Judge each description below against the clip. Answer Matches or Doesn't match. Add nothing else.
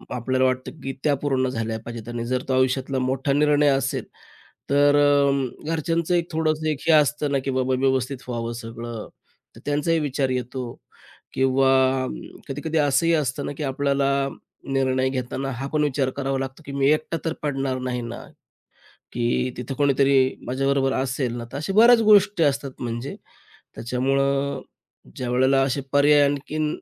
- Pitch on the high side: Doesn't match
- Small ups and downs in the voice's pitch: Matches